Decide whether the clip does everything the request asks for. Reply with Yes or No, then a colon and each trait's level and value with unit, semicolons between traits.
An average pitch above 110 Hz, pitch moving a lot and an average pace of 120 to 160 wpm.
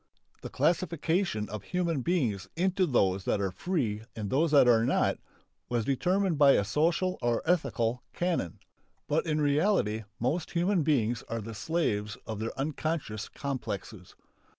Yes: medium, 140 Hz; wide, 7.5 semitones; average, 150 wpm